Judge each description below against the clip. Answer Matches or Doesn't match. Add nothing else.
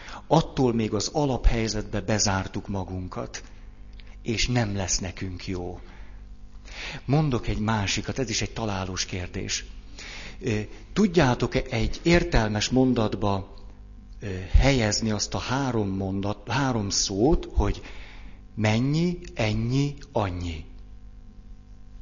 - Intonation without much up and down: Doesn't match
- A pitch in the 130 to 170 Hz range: Doesn't match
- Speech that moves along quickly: Doesn't match